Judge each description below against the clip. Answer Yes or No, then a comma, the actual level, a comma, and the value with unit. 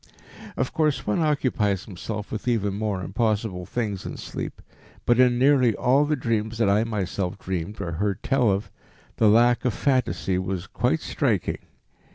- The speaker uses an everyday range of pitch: Yes, average, 4.1 semitones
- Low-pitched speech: Yes, low, 110 Hz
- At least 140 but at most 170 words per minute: Yes, average, 165 wpm